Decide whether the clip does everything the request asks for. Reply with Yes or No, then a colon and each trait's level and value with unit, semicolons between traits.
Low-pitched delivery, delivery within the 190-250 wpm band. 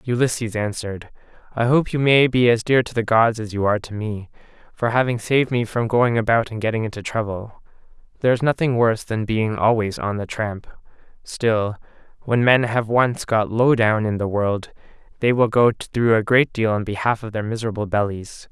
Yes: low, 115 Hz; average, 200 wpm